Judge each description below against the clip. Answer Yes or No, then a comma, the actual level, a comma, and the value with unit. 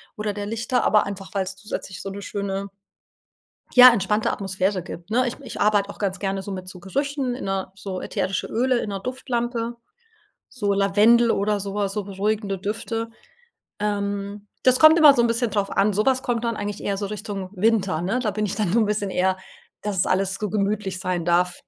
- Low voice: No, high, 205 Hz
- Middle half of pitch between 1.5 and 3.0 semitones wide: Yes, average, 2.7 semitones